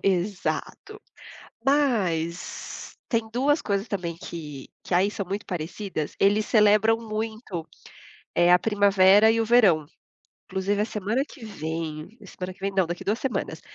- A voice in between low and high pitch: No, high, 200 Hz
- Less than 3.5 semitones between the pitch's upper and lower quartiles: No, average, 3.8 semitones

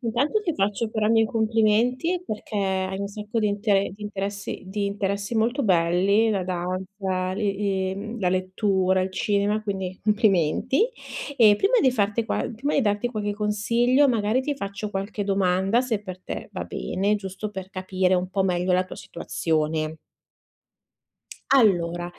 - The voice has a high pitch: Yes, high, 200 Hz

